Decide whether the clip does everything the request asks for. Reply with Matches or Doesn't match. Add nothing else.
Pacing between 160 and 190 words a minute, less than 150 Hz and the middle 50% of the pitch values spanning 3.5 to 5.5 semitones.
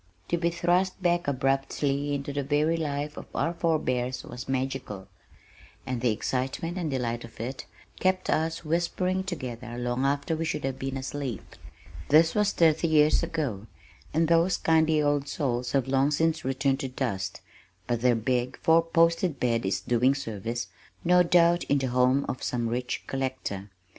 Matches